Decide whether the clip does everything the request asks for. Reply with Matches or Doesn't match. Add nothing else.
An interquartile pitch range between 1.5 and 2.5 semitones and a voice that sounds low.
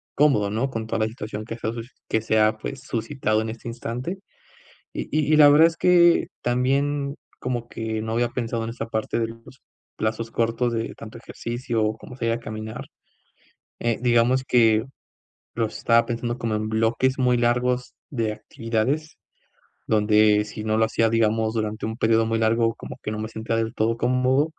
Matches